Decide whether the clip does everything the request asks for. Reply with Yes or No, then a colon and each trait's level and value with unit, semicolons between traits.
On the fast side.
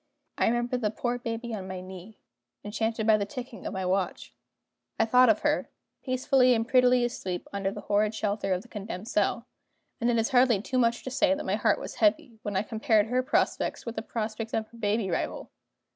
Yes: fast, 210 wpm